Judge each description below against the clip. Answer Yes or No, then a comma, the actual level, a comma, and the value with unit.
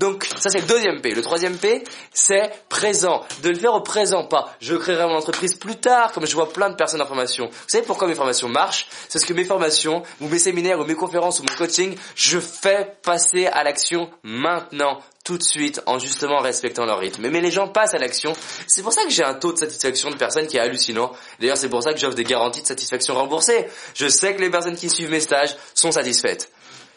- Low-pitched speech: No, medium, 170 Hz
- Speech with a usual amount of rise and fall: Yes, average, 4.6 semitones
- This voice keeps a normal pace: No, fast, 240 wpm